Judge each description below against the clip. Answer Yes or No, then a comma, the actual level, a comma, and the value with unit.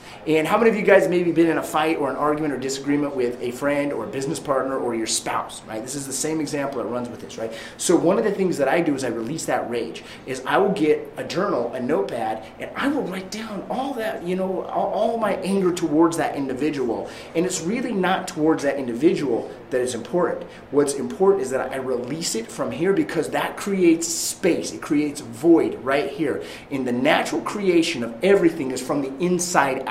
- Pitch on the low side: No, medium, 155 Hz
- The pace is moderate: No, fast, 230 wpm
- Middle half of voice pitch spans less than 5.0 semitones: No, wide, 5.6 semitones